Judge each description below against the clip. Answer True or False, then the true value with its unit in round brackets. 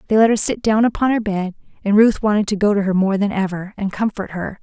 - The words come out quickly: True (270 wpm)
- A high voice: True (205 Hz)